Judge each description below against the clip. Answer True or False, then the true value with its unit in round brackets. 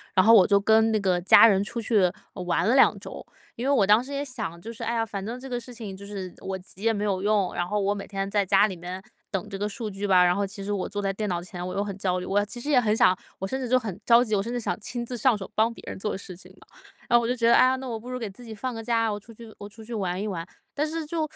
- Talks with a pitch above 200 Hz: True (210 Hz)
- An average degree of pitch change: True (3.2 semitones)